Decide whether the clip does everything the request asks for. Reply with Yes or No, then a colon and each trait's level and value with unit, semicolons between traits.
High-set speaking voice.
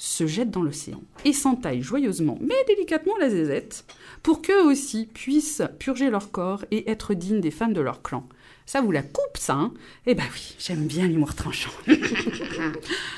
Yes: high, 235 Hz